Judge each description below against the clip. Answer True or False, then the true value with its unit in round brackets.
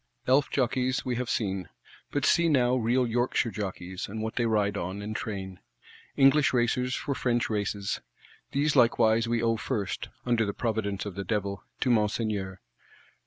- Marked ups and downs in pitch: False (3.7 semitones)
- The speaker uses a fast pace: False (165 wpm)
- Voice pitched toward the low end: True (115 Hz)